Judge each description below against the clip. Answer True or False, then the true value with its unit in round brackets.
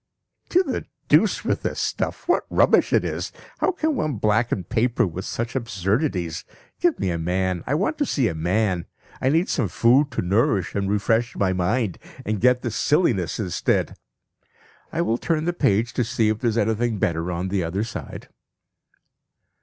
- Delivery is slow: False (180 wpm)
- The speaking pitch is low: True (110 Hz)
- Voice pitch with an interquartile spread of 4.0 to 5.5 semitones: True (5.2 semitones)